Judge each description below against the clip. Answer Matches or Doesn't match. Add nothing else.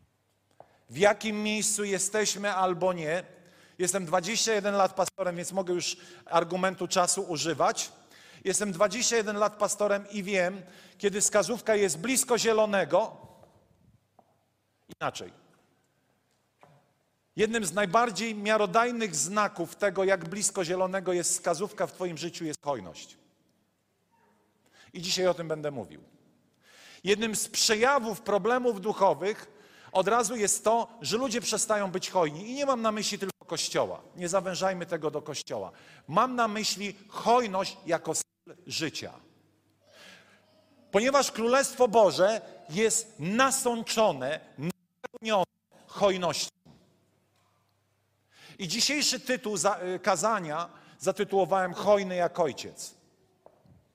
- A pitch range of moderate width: Matches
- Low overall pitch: Doesn't match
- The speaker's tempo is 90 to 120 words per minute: Matches